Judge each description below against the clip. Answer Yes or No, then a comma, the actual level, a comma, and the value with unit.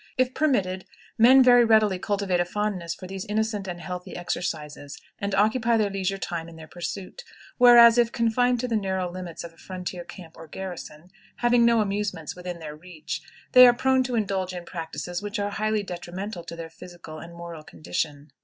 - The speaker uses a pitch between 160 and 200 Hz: Yes, high, 190 Hz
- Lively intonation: No, average, 4.1 semitones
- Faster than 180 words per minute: Yes, average, 190 wpm